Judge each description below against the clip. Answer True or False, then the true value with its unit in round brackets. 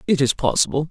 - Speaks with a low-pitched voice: False (150 Hz)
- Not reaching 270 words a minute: True (200 wpm)